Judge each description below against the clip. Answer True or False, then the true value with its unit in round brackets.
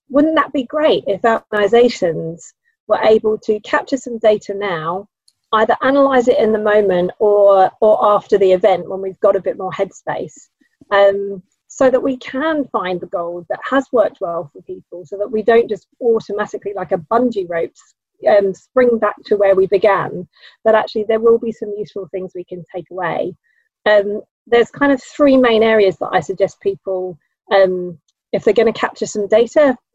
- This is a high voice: True (210 Hz)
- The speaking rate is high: False (185 wpm)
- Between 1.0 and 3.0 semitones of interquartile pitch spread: False (3.6 semitones)